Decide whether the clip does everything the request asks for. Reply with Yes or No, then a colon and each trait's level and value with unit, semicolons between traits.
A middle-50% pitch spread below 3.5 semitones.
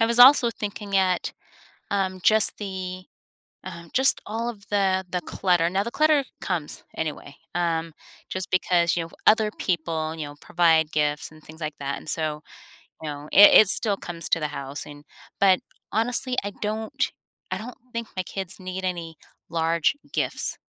No: average, 4.3 semitones